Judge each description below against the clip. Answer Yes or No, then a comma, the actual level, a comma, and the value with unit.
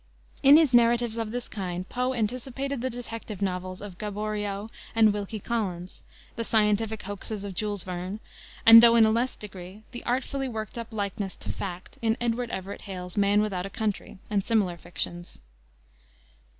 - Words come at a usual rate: Yes, average, 165 wpm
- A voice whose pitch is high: Yes, high, 215 Hz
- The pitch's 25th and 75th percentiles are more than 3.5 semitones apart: No, average, 3.2 semitones